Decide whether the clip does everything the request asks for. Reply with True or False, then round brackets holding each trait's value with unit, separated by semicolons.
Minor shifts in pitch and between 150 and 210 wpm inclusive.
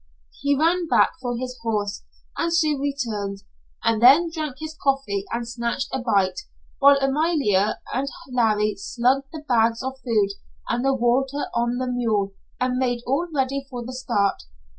False (3.4 semitones; 160 wpm)